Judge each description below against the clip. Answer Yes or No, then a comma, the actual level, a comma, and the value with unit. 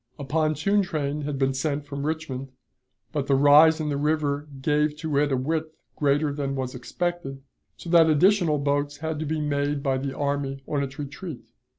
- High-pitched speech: No, medium, 145 Hz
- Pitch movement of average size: No, narrow, 2.0 semitones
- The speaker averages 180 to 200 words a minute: Yes, average, 190 wpm